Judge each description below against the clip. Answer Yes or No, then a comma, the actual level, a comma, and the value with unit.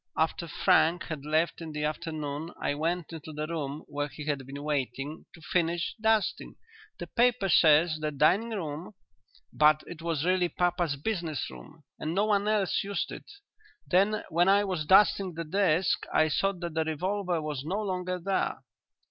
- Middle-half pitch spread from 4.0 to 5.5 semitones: No, average, 3.6 semitones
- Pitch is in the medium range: Yes, medium, 165 Hz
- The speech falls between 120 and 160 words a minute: No, average, 175 wpm